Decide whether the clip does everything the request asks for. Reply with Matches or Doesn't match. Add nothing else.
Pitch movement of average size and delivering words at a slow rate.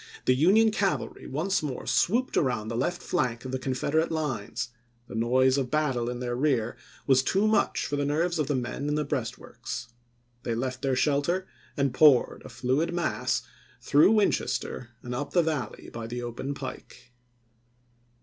Doesn't match